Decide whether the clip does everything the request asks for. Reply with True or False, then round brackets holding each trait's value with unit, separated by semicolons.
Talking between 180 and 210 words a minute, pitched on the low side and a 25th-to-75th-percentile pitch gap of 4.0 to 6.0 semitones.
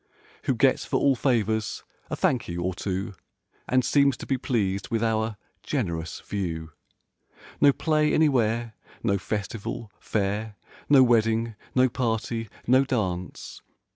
False (135 wpm; 110 Hz; 4.3 semitones)